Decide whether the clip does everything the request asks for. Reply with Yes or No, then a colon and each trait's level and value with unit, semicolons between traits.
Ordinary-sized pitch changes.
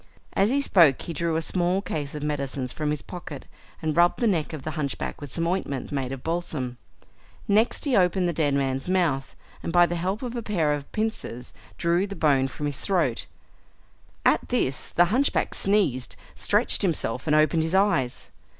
Yes: average, 4.8 semitones